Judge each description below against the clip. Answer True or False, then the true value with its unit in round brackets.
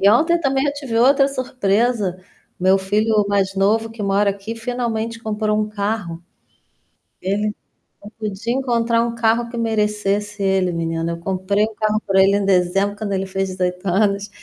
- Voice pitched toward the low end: False (210 Hz)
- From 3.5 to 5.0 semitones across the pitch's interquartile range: False (2.8 semitones)